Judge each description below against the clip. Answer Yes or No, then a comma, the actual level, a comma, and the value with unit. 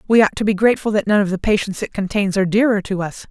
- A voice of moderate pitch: No, high, 205 Hz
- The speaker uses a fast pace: Yes, fast, 290 wpm